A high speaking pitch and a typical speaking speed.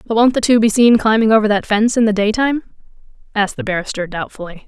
No: high, 220 Hz; fast, 220 wpm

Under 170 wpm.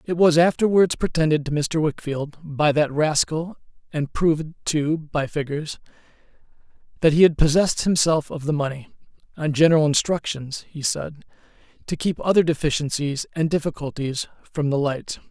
Yes: slow, 135 wpm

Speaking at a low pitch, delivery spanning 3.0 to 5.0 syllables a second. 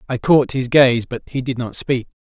Yes: low, 125 Hz; 4.8 syllables/s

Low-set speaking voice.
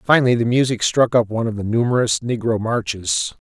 Yes: low, 115 Hz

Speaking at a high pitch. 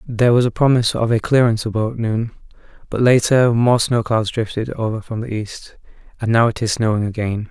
No: low, 115 Hz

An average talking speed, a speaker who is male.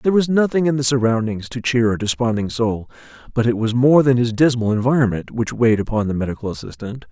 No: fast, 210 wpm; male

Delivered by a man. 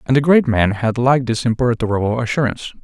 Yes: male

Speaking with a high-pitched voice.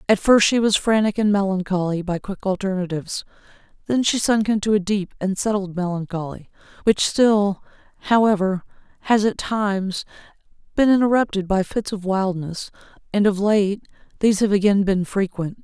Yes: high, 200 Hz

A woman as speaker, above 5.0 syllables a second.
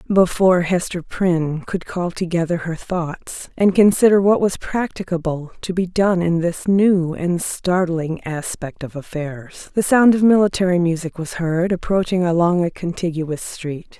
No: female; 4.3 syllables/s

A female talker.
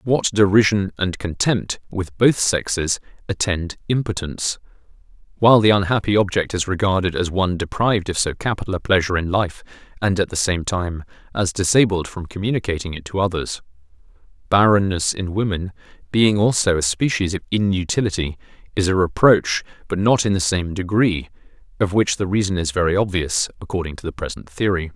No: male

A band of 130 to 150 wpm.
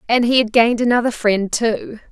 No: average, 200 wpm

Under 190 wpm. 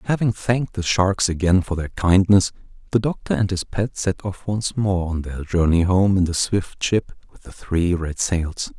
No: fast, 205 wpm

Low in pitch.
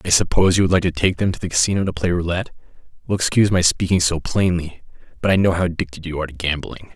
Yes: very low, 85 Hz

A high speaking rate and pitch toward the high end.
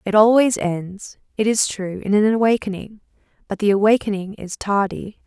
No: average, 160 wpm; high, 205 Hz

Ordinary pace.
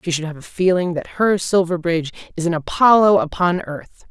Yes: average, 190 wpm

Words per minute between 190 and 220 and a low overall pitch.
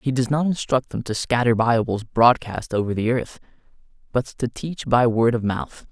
Yes: average, 195 wpm; low, 120 Hz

